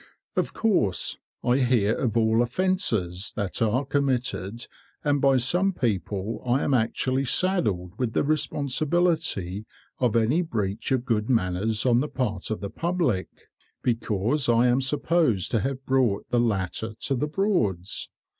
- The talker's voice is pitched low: Yes, low, 120 Hz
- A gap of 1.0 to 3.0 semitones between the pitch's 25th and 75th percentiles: No, average, 4.7 semitones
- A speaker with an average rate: Yes, average, 145 wpm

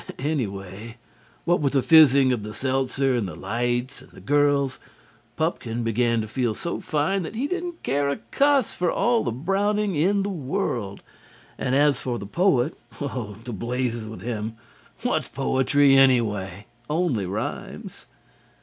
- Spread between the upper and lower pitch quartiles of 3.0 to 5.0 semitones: No, wide, 5.4 semitones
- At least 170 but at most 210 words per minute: No, average, 155 wpm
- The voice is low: Yes, low, 130 Hz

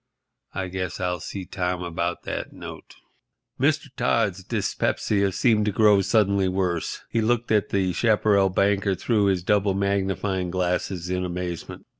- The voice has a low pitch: Yes, very low, 95 Hz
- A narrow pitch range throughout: Yes, narrow, 2.1 semitones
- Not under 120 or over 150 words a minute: Yes, average, 145 wpm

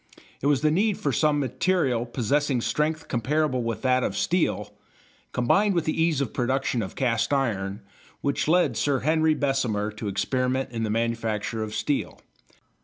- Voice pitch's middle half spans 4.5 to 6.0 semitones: Yes, average, 4.8 semitones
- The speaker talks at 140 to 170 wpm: Yes, average, 165 wpm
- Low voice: Yes, low, 130 Hz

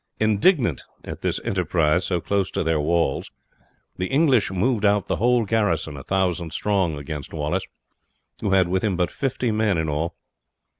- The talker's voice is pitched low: Yes, very low, 95 Hz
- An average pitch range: Yes, average, 4.7 semitones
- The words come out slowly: No, average, 160 wpm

